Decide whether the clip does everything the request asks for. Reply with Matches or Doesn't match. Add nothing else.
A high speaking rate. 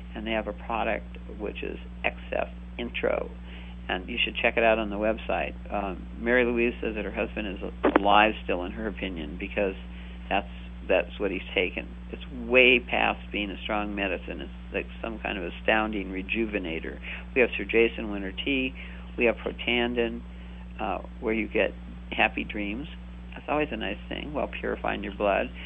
Doesn't match